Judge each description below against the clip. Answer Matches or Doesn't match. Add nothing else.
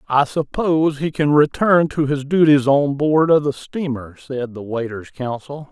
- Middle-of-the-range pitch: Matches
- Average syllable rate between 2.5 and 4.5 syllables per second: Matches